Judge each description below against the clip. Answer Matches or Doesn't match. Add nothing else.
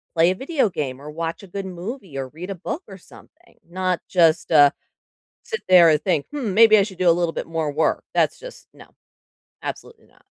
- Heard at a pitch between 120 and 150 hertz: Doesn't match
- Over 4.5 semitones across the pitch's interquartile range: Doesn't match